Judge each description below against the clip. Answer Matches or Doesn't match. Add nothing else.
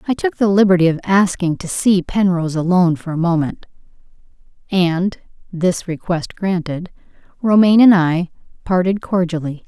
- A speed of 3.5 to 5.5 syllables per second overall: Matches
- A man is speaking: Doesn't match